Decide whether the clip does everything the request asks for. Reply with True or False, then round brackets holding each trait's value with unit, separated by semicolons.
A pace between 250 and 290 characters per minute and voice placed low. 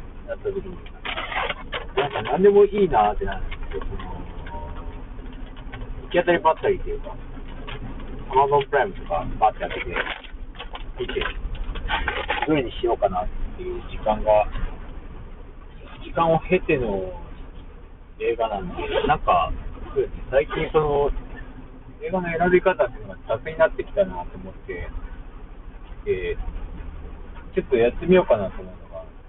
False (260 characters per minute; 145 Hz)